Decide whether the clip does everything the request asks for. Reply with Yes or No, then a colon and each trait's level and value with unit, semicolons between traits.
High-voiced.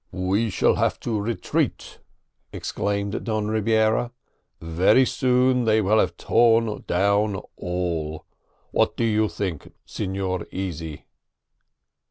No: low, 105 Hz